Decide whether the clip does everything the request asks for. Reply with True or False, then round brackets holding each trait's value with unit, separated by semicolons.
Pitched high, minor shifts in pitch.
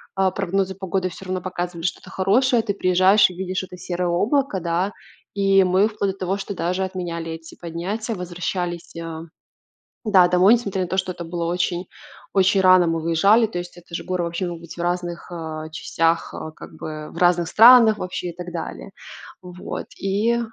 False (180 Hz; 2.1 semitones)